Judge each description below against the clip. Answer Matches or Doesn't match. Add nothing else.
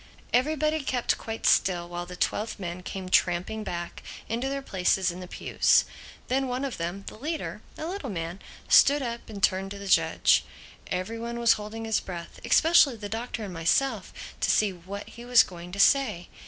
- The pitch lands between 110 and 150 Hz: Doesn't match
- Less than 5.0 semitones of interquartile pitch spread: Doesn't match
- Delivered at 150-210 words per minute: Matches